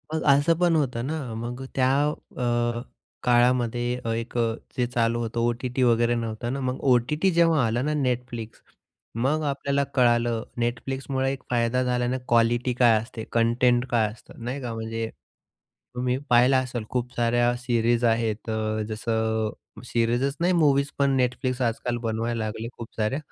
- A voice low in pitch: Yes, low, 120 Hz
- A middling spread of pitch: No, narrow, 2.0 semitones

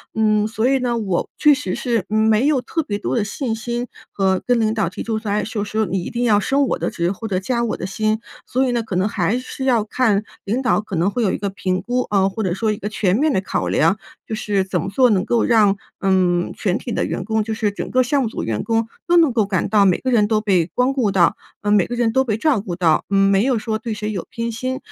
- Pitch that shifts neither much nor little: Yes, average, 3.5 semitones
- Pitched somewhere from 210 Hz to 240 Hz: Yes, high, 215 Hz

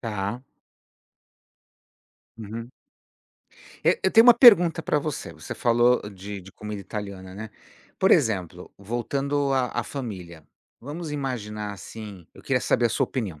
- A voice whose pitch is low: Yes, low, 115 Hz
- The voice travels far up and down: Yes, wide, 5.7 semitones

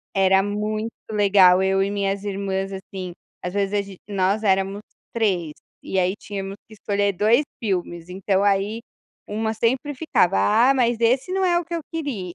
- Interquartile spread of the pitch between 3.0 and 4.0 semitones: No, narrow, 2.5 semitones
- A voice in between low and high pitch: No, high, 200 Hz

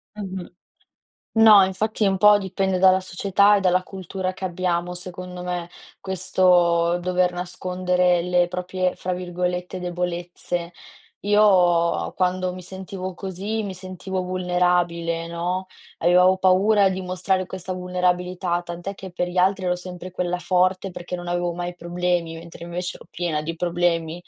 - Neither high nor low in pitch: Yes, medium, 180 Hz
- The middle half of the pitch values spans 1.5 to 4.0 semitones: No, narrow, 1.1 semitones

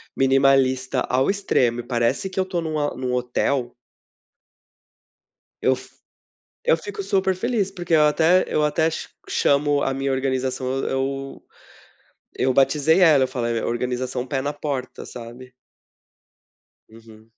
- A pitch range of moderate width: Yes, average, 3.9 semitones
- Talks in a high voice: No, low, 135 Hz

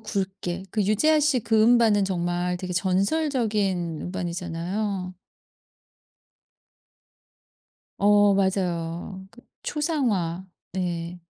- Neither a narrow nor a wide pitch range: Yes, average, 3.4 semitones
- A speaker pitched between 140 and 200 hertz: Yes, high, 190 Hz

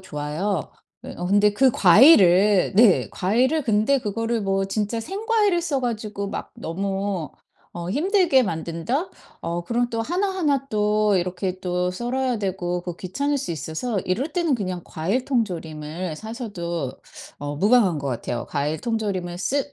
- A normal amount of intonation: No, wide, 6.0 semitones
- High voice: Yes, high, 205 Hz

